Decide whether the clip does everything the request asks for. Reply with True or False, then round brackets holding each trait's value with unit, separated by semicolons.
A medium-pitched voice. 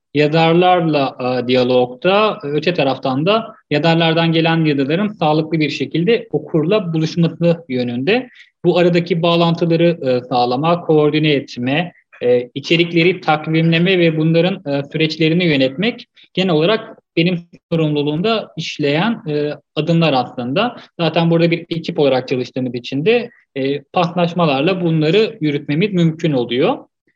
True (160 Hz)